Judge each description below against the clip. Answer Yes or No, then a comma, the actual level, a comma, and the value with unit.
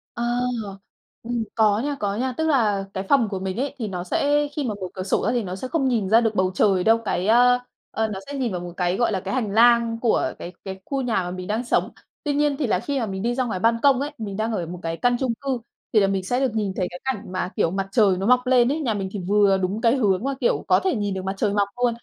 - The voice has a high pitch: Yes, high, 220 Hz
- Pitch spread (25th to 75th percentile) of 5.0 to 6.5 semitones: No, average, 4.4 semitones